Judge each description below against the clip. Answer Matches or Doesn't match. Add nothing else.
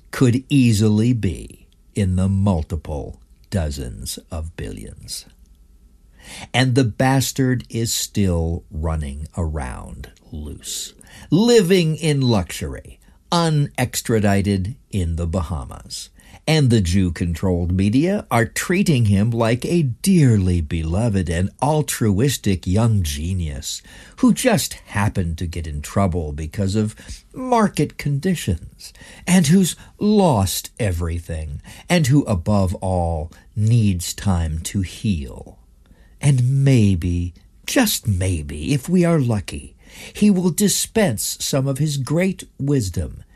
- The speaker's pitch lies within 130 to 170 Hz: Doesn't match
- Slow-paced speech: Matches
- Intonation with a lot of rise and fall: Matches